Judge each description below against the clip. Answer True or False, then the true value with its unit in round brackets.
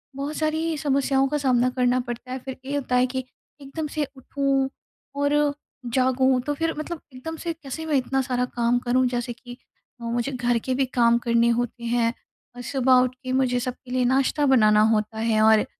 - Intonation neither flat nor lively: False (2.3 semitones)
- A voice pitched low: False (255 Hz)